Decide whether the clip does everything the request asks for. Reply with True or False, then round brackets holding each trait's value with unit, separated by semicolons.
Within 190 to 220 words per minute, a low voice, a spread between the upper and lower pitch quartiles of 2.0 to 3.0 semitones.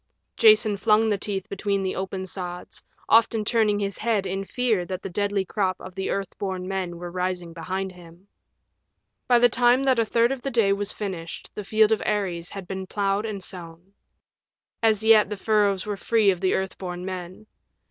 False (195 wpm; 195 Hz; 2.6 semitones)